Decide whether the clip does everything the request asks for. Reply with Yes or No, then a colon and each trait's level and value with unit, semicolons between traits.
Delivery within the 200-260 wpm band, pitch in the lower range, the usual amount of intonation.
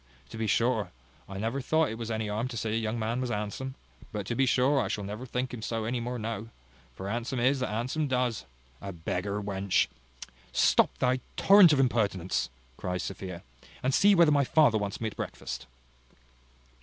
Yes: fast, 205 wpm; low, 115 Hz; average, 3.7 semitones